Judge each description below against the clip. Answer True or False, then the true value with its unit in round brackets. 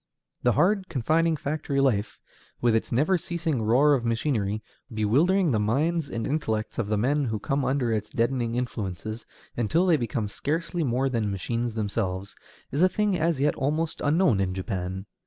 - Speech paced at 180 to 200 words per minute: False (170 wpm)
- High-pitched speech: False (125 Hz)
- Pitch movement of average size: False (6.1 semitones)